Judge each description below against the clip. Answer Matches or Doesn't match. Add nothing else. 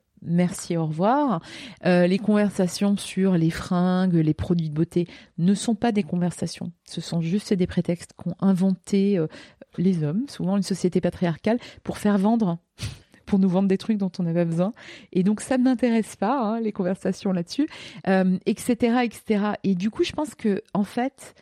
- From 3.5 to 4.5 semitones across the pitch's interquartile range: Doesn't match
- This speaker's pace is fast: Doesn't match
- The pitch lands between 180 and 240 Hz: Matches